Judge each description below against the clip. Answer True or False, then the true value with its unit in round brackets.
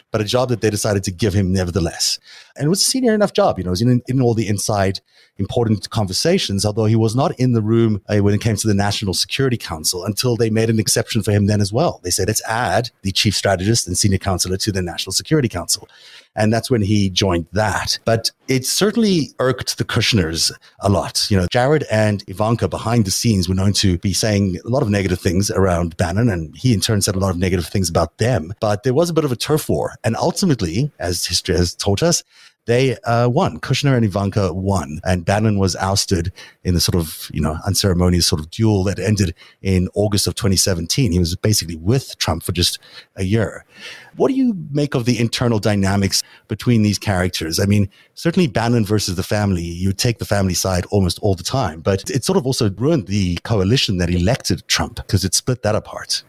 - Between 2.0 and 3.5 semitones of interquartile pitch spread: False (3.9 semitones)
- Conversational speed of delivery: False (220 wpm)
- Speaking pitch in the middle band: False (105 Hz)